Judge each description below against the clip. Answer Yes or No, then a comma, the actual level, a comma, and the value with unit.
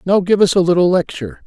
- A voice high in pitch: No, medium, 180 Hz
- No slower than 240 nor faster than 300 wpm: Yes, fast, 245 wpm